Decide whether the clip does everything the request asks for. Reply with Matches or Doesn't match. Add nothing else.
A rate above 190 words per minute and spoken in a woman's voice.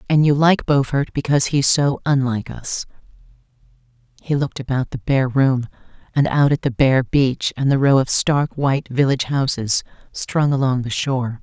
Doesn't match